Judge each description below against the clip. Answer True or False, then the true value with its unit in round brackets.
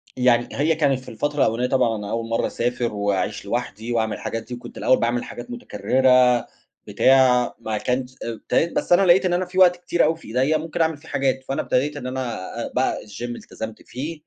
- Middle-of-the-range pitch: False (125 Hz)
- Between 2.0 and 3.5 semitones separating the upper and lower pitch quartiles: False (4.3 semitones)